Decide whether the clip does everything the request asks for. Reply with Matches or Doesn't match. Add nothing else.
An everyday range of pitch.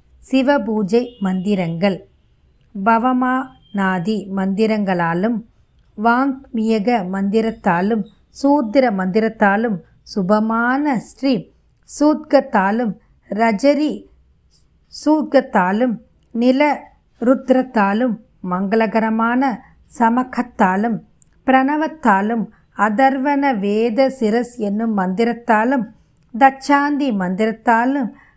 Matches